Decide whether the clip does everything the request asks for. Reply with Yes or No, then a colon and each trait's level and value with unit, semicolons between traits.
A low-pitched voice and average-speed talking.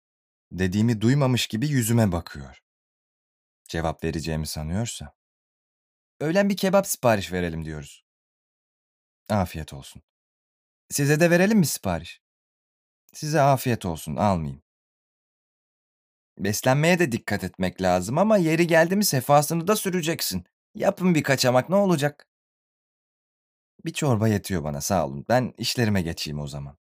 Yes: low, 115 Hz; average, 120 wpm